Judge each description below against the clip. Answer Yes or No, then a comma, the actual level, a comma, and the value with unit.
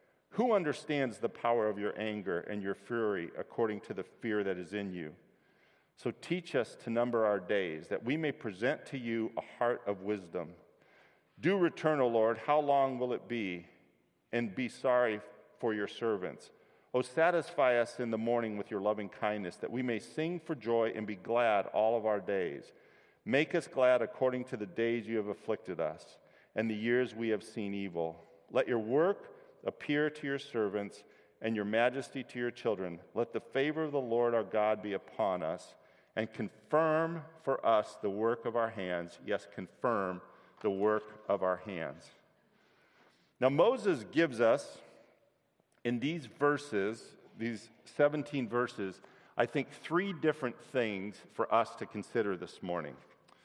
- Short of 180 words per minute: Yes, average, 170 wpm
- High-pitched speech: No, low, 115 Hz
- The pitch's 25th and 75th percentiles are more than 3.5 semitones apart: Yes, average, 4.7 semitones